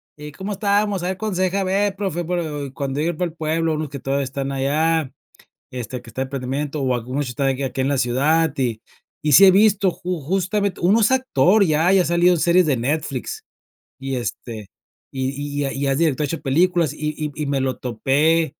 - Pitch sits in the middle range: Yes, medium, 150 Hz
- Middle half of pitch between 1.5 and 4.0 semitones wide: No, average, 4.8 semitones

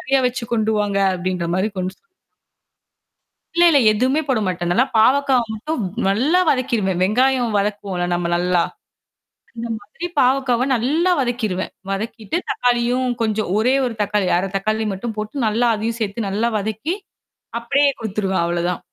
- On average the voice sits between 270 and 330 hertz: No, high, 220 Hz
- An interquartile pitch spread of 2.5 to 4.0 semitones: No, average, 4.5 semitones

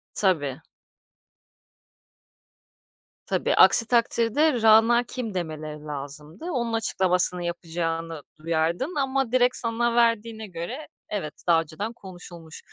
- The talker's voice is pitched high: Yes, high, 195 Hz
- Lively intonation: Yes, wide, 6.3 semitones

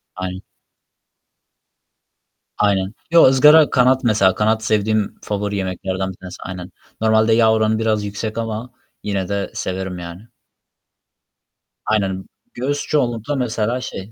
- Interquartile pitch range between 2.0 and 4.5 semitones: Yes, average, 3.2 semitones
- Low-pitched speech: Yes, low, 110 Hz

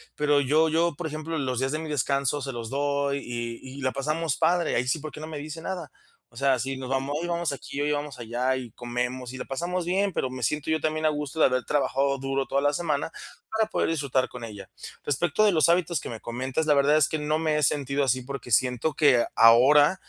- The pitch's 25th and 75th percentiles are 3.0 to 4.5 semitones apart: Yes, average, 3.3 semitones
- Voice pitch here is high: No, medium, 140 Hz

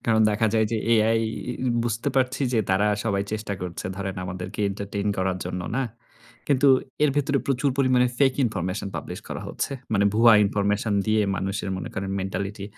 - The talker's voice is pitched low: Yes, low, 105 Hz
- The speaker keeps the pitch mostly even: No, average, 3.4 semitones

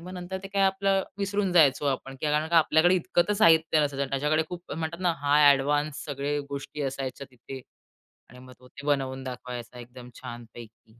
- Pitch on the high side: No, medium, 145 Hz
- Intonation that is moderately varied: Yes, average, 4.2 semitones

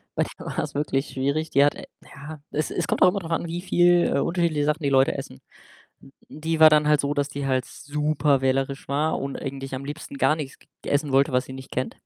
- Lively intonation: No, narrow, 2.5 semitones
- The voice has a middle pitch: Yes, medium, 145 Hz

